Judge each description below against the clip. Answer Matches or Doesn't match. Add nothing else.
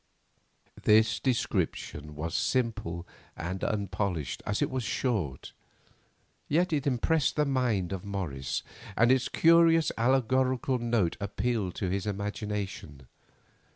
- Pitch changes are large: Matches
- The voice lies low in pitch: Matches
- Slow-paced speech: Matches